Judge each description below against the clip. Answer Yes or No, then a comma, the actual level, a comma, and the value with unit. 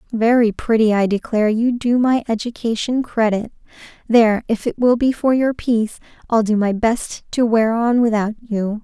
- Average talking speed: Yes, average, 170 wpm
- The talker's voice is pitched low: No, high, 225 Hz